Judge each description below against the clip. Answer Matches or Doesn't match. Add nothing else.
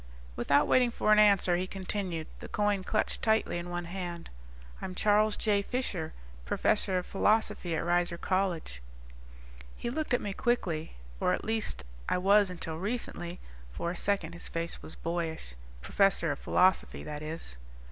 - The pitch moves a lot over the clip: Doesn't match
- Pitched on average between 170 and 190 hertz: Matches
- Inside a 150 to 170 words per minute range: Matches